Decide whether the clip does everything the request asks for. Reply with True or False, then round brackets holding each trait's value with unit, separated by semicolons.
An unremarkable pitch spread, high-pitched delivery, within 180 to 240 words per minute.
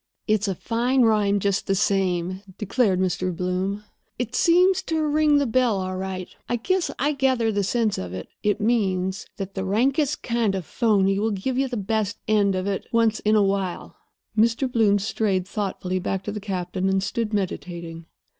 True (3.7 semitones; 205 Hz; 190 wpm)